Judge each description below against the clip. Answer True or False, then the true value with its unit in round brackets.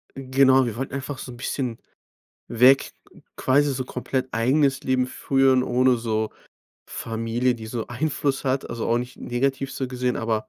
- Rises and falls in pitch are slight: True (2.2 semitones)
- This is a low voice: True (130 Hz)